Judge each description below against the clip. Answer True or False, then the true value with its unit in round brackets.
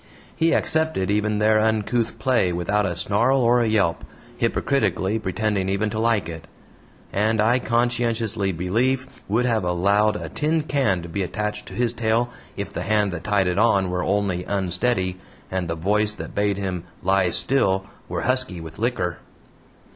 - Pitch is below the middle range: True (105 Hz)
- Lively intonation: False (3.8 semitones)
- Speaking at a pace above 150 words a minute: True (170 wpm)